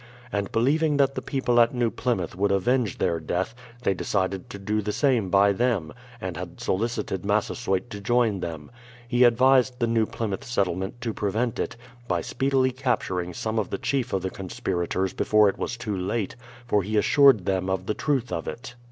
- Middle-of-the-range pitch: No, low, 105 Hz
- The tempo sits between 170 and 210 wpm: Yes, average, 190 wpm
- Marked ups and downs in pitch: No, average, 4.3 semitones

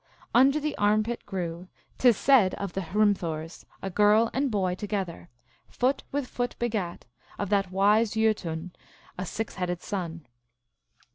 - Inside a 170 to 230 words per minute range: No, average, 150 wpm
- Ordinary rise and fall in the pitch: Yes, average, 3.8 semitones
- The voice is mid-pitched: No, high, 205 Hz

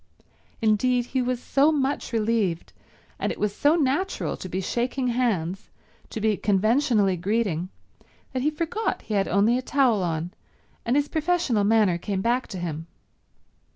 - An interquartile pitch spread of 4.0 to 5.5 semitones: Yes, average, 5.1 semitones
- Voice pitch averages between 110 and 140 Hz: No, high, 225 Hz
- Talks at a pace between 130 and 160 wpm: Yes, average, 155 wpm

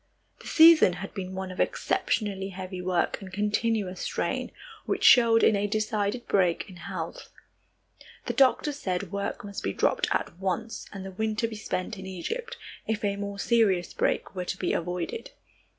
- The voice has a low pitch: No, high, 200 Hz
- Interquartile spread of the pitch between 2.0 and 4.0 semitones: Yes, average, 2.9 semitones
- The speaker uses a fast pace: No, average, 170 wpm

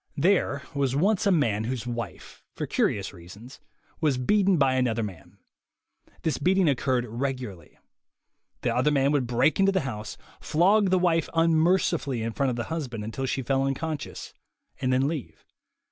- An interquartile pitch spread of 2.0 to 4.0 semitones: No, wide, 5.4 semitones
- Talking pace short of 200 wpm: Yes, average, 165 wpm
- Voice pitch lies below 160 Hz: Yes, low, 135 Hz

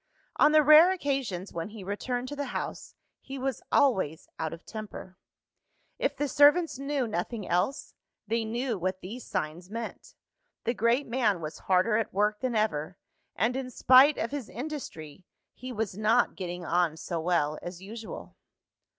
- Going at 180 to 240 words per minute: No, average, 165 wpm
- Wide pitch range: Yes, wide, 6.3 semitones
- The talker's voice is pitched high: Yes, high, 220 Hz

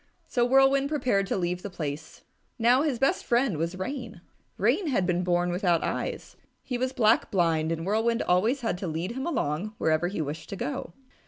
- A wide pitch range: Yes, wide, 6.2 semitones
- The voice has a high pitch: Yes, high, 195 Hz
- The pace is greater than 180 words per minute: Yes, average, 190 wpm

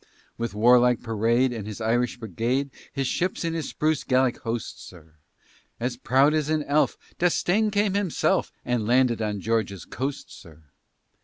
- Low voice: Yes, low, 125 Hz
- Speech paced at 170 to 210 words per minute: No, average, 155 wpm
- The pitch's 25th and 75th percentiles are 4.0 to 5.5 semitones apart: Yes, average, 4.6 semitones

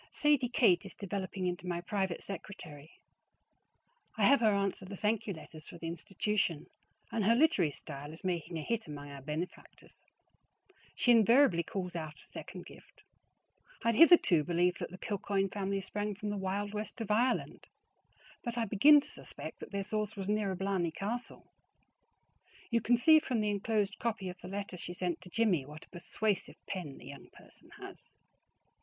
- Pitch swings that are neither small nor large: Yes, average, 3.8 semitones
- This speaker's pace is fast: No, average, 180 wpm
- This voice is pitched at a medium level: No, high, 195 Hz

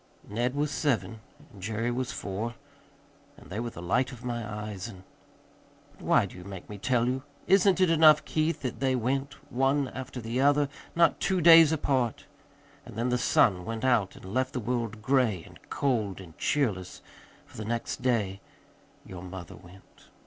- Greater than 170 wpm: Yes, average, 180 wpm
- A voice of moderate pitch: No, low, 120 Hz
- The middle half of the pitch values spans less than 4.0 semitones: No, average, 4.6 semitones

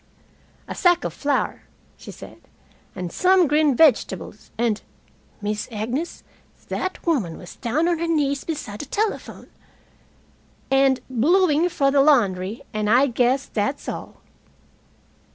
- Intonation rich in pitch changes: Yes, wide, 6.5 semitones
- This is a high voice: Yes, very high, 275 Hz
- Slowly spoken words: Yes, slow, 130 wpm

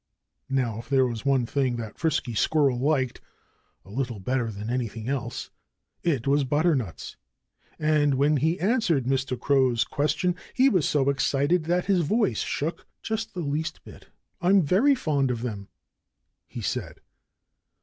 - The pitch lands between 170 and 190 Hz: No, medium, 140 Hz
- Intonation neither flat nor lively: Yes, average, 4.6 semitones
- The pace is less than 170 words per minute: Yes, average, 150 wpm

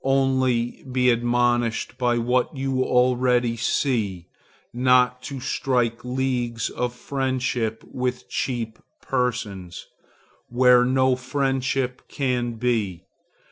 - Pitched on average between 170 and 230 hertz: No, low, 125 Hz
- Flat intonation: Yes, narrow, 1.5 semitones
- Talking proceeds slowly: Yes, slow, 100 wpm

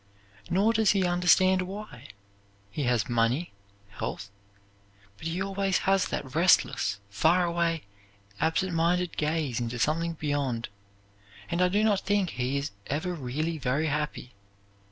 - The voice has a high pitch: No, medium, 165 Hz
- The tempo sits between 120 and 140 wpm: Yes, slow, 135 wpm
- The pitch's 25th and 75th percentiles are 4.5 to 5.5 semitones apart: Yes, average, 5.1 semitones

